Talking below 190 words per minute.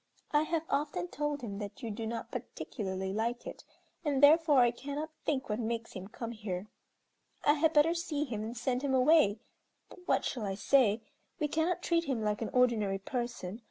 No: average, 195 wpm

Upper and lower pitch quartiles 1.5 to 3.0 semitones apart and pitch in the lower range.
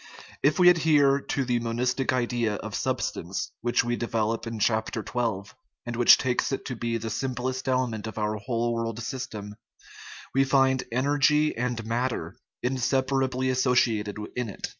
Yes: narrow, 2.4 semitones; low, 120 Hz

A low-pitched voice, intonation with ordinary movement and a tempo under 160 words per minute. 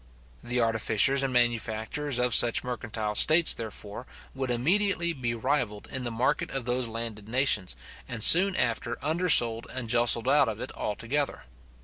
Yes: low, 120 Hz; average, 3.2 semitones; average, 150 wpm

